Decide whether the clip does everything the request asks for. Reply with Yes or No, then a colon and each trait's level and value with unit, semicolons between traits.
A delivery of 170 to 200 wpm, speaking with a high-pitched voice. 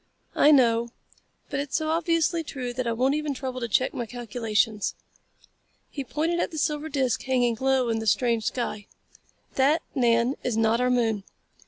Yes: average, 175 wpm; very high, 255 Hz